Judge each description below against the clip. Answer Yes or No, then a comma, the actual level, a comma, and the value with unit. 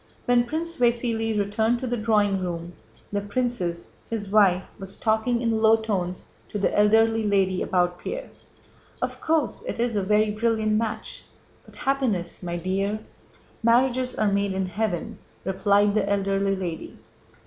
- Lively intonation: No, average, 3.0 semitones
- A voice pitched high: Yes, high, 210 Hz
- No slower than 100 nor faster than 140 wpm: No, average, 150 wpm